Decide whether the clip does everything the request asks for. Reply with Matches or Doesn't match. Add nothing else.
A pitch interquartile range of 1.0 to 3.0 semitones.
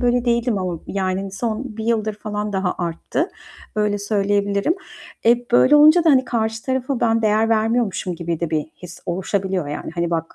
Doesn't match